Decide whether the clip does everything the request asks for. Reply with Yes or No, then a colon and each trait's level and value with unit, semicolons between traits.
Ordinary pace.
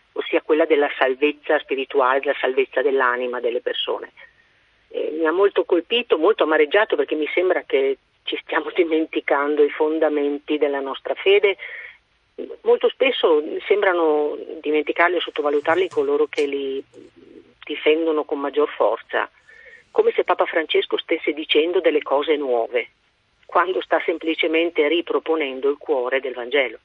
Yes: average, 130 wpm